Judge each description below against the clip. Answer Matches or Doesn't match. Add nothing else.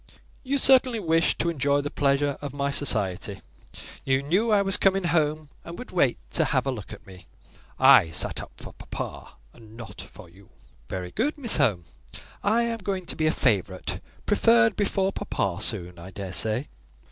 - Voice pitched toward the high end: Doesn't match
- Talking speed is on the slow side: Doesn't match